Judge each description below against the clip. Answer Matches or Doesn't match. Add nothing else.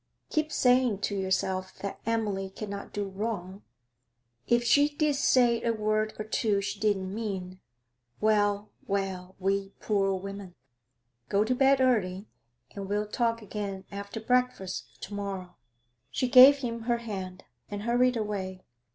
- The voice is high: Matches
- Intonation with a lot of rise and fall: Doesn't match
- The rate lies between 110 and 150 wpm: Matches